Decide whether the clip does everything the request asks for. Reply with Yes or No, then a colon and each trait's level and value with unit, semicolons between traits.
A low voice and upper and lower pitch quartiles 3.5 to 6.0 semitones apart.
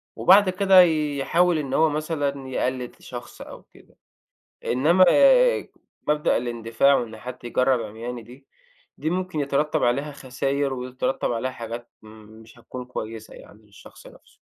Yes: low, 130 Hz; average, 4.1 semitones